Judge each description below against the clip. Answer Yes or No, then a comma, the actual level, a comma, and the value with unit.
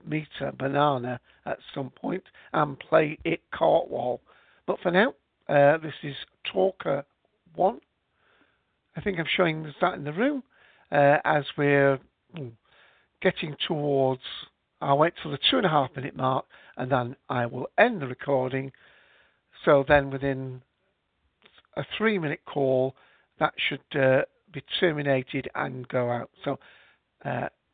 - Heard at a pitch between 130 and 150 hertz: Yes, medium, 140 Hz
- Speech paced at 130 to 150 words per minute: Yes, average, 140 wpm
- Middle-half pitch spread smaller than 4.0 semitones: Yes, average, 2.8 semitones